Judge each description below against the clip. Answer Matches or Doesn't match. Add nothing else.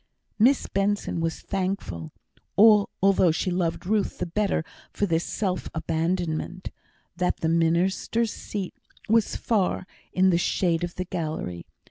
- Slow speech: Matches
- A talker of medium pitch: Matches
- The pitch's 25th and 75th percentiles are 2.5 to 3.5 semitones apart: Matches